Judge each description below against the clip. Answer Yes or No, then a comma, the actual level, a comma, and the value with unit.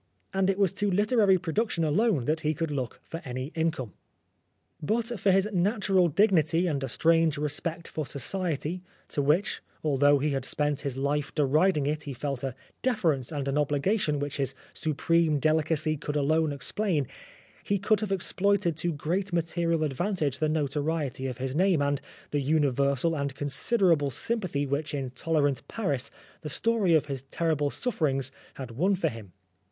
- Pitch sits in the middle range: Yes, medium, 155 Hz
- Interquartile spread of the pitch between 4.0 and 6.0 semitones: Yes, average, 4.4 semitones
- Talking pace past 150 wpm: Yes, average, 165 wpm